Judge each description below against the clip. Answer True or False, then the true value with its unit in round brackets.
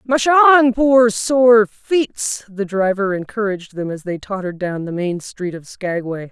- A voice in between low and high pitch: False (210 Hz)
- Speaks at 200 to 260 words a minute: False (170 wpm)